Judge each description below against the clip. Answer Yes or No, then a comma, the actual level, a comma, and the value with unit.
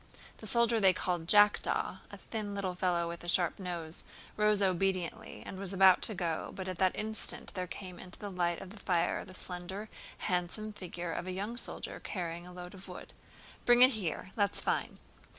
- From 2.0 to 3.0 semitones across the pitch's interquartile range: Yes, average, 2.7 semitones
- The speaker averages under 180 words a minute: No, average, 190 wpm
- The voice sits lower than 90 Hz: No, medium, 185 Hz